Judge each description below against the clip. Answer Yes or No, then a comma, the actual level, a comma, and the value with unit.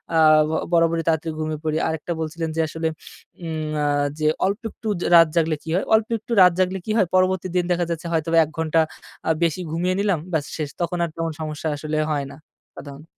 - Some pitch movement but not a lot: No, narrow, 2.3 semitones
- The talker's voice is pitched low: No, medium, 165 Hz